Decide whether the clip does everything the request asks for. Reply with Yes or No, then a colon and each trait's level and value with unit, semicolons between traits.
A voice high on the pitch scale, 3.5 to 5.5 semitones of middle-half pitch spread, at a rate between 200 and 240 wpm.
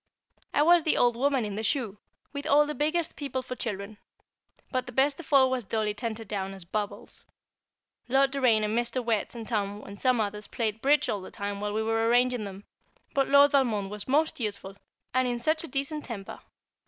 Yes: high, 235 Hz; average, 4.7 semitones; fast, 205 wpm